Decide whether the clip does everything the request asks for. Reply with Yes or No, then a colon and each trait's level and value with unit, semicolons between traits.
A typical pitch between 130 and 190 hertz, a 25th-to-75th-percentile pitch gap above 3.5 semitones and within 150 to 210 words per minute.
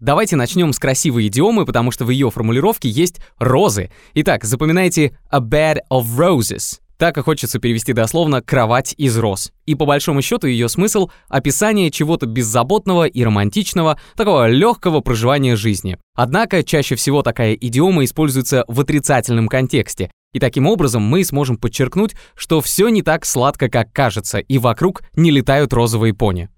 Yes: low, 135 Hz; average, 5.2 semitones; average, 155 wpm